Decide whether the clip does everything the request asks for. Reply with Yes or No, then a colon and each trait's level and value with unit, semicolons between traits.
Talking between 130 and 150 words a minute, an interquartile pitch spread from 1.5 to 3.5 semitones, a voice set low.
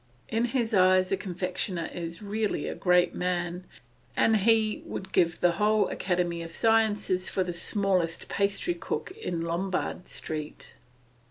No: average, 140 wpm; average, 3.2 semitones; medium, 185 Hz